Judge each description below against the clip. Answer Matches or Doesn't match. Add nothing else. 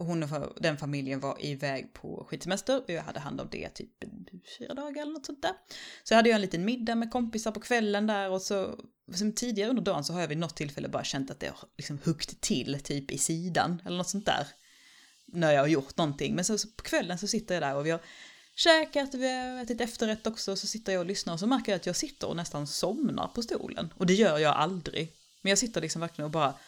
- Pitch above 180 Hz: Matches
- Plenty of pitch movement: Matches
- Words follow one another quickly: Matches